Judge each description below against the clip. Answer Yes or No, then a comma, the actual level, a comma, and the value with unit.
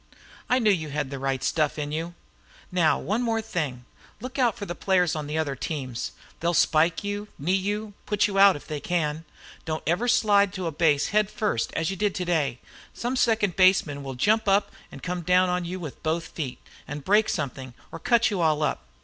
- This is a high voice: No, medium, 175 Hz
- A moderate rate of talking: No, fast, 210 wpm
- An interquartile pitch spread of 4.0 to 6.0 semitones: Yes, average, 5.2 semitones